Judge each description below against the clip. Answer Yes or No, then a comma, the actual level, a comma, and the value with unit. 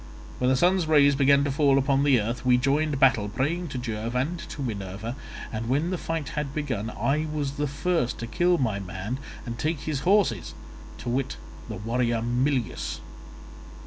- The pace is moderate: Yes, average, 175 wpm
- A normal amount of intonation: Yes, average, 4.1 semitones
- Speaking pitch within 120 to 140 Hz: Yes, low, 135 Hz